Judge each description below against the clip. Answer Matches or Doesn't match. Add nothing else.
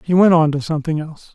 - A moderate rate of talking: Doesn't match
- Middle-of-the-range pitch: Matches